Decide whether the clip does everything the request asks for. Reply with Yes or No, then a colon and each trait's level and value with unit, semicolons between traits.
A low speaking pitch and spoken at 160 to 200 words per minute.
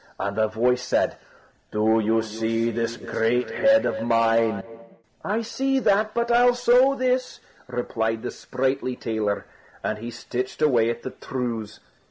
No: low, 120 Hz; average, 150 wpm